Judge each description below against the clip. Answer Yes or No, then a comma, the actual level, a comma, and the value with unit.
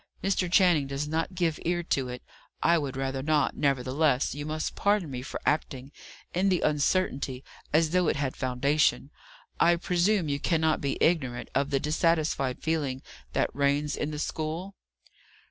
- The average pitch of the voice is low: No, medium, 150 Hz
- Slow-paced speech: No, average, 165 wpm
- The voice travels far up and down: No, average, 3.6 semitones